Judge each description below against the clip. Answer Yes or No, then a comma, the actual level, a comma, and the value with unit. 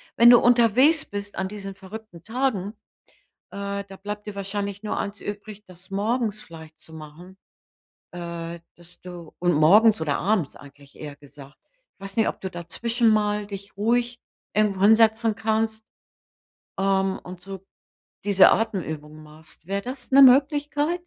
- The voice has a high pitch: Yes, high, 200 Hz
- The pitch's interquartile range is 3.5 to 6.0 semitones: Yes, average, 4.0 semitones